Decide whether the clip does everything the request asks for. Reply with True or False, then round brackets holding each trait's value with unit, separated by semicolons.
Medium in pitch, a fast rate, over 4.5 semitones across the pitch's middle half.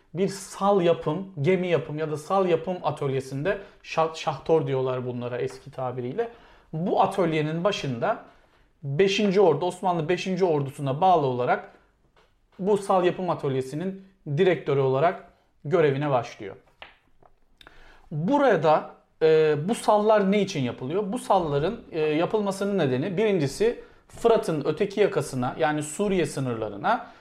False (170 Hz; 115 wpm; 5.5 semitones)